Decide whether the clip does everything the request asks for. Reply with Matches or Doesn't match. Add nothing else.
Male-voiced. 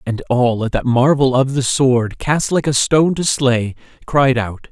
Matches